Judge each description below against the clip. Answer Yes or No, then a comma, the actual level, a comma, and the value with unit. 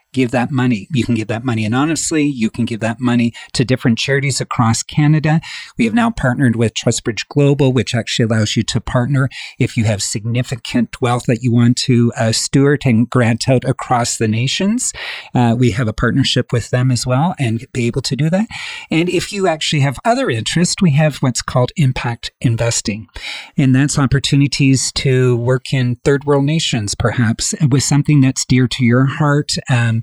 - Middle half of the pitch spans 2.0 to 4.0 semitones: Yes, average, 3.3 semitones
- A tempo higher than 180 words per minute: Yes, average, 190 wpm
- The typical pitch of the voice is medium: No, low, 130 Hz